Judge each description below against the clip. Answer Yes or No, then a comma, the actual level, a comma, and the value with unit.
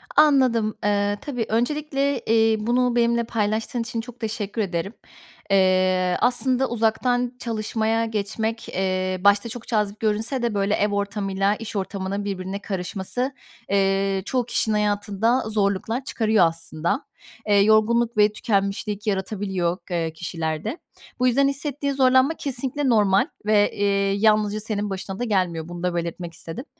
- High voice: Yes, high, 210 Hz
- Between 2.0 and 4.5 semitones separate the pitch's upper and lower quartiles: Yes, average, 3.3 semitones